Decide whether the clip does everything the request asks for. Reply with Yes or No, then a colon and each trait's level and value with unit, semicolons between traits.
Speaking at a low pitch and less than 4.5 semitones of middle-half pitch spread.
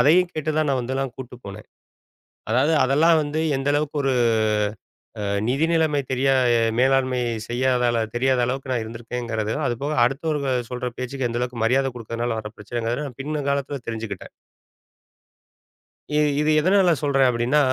Yes: low, 130 Hz; average, 3.3 semitones